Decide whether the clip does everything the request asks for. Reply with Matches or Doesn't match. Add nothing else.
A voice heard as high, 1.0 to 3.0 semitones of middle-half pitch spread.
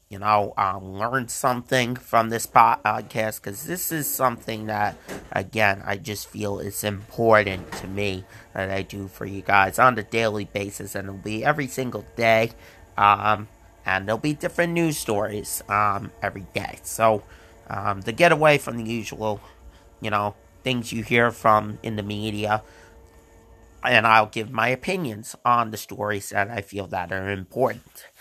Doesn't match